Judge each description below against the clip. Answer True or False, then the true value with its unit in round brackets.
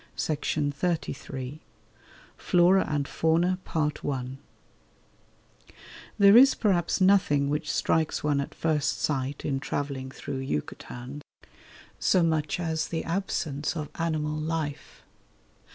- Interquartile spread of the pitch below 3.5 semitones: True (3.0 semitones)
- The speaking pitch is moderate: True (155 Hz)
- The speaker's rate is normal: False (105 wpm)